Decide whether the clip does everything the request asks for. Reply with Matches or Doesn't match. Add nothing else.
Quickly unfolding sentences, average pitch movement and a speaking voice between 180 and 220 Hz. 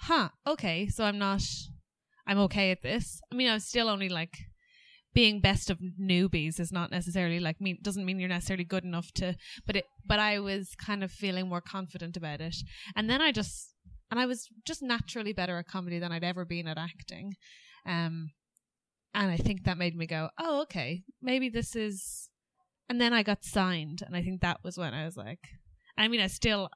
Matches